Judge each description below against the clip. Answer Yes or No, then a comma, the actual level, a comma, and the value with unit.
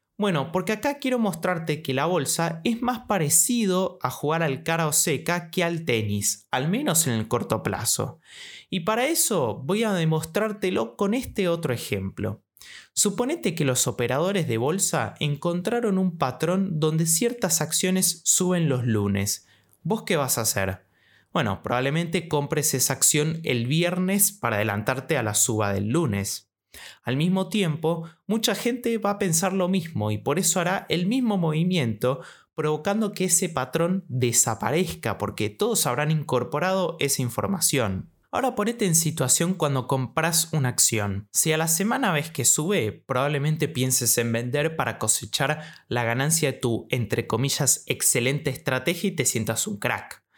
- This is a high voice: No, medium, 155 Hz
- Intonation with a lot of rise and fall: Yes, wide, 6.9 semitones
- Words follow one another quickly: No, average, 155 wpm